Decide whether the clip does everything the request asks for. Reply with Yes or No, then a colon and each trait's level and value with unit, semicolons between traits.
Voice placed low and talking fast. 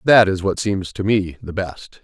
Yes: very low, 95 Hz; fast, 235 wpm